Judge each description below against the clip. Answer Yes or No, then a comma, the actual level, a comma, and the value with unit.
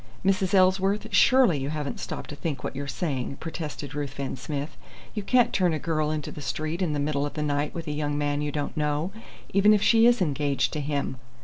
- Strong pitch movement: No, average, 4.1 semitones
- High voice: No, medium, 150 Hz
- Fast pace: Yes, fast, 220 wpm